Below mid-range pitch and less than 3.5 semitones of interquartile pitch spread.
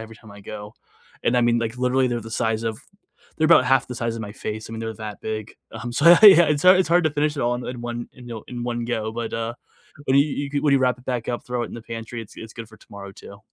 Yes: low, 120 Hz; narrow, 2.6 semitones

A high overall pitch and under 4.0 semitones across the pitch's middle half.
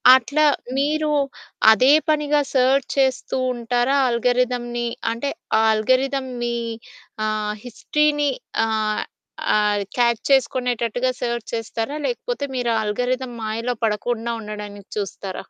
Yes: high, 245 Hz; average, 3.2 semitones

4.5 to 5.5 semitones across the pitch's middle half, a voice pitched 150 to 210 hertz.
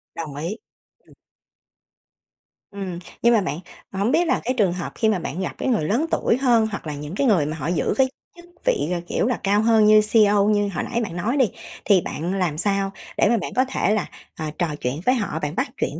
Yes: average, 5.2 semitones; high, 200 Hz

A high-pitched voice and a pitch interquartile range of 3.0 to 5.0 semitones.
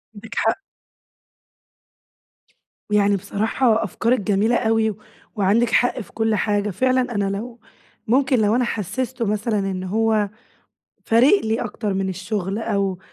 No: high, 220 Hz; narrow, 2.5 semitones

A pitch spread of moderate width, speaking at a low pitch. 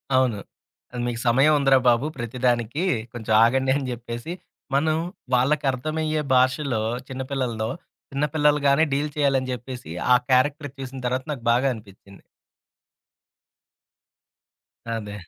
Yes: average, 3.2 semitones; low, 130 Hz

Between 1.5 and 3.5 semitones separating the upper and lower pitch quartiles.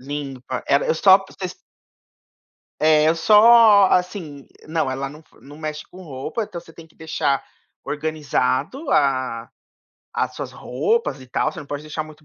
No: average, 4.2 semitones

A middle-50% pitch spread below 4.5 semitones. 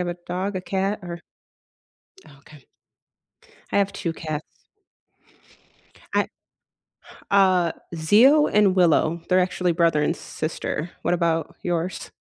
Yes: average, 2.7 semitones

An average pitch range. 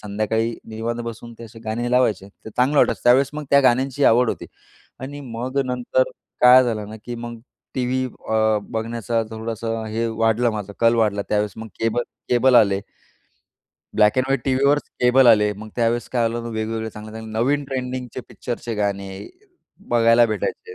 No: narrow, 2.3 semitones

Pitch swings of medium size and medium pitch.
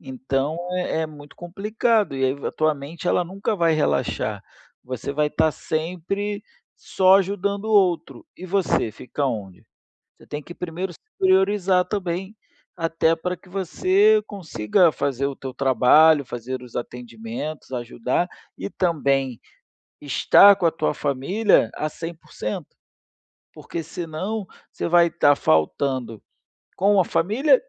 No: wide, 5.8 semitones; medium, 165 Hz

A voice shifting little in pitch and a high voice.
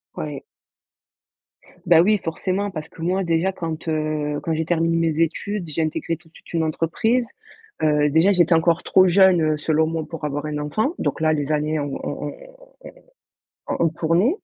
No: narrow, 2.3 semitones; medium, 165 Hz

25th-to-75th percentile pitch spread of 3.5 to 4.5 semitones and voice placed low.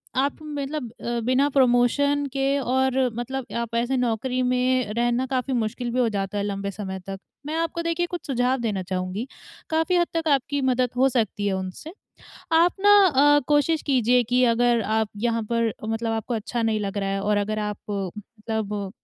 No: average, 3.9 semitones; high, 245 Hz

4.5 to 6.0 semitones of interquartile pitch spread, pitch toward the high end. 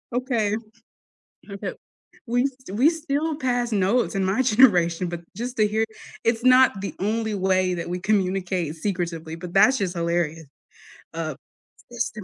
Yes: wide, 5.5 semitones; high, 205 Hz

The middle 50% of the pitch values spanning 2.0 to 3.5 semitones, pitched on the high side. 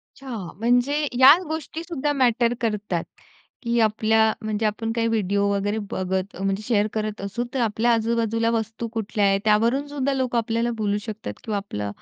Yes: narrow, 2.5 semitones; high, 225 Hz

